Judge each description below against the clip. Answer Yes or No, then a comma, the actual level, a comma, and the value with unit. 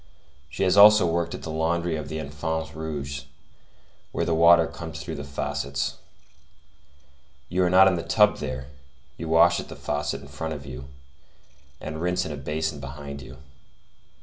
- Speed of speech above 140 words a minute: Yes, average, 170 wpm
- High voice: No, very low, 80 Hz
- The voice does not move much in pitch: No, average, 3.2 semitones